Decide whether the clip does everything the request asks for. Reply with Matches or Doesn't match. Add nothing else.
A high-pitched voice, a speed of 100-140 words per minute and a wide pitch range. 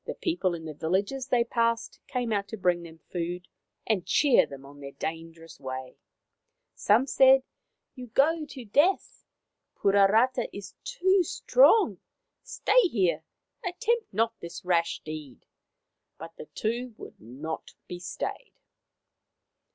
Matches